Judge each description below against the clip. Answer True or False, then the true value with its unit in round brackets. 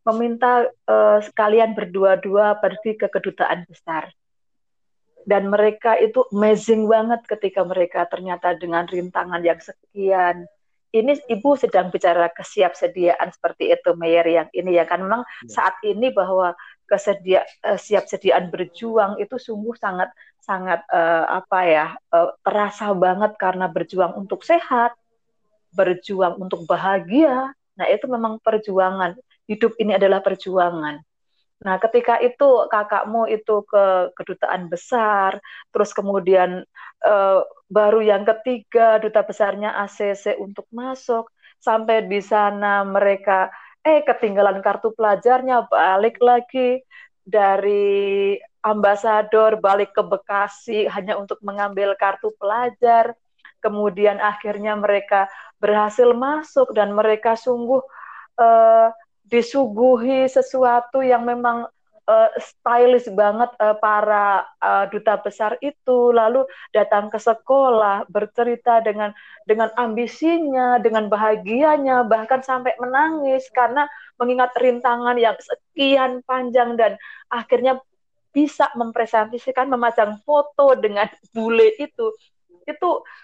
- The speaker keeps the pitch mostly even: False (3.7 semitones)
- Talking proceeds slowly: False (110 wpm)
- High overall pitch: True (215 Hz)